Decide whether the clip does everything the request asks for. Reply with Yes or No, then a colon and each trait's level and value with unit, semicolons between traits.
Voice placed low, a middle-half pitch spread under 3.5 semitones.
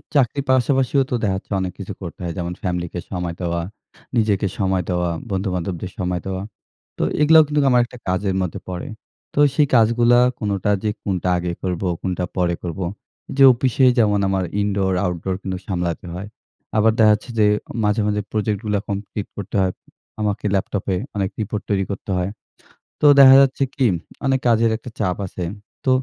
No: low, 100 Hz; average, 3.8 semitones